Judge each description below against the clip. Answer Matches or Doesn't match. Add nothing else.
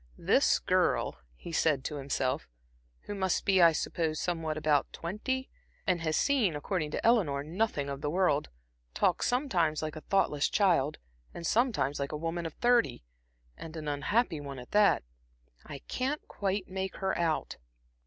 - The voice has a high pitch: Doesn't match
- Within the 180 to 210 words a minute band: Doesn't match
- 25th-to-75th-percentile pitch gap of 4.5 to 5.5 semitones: Matches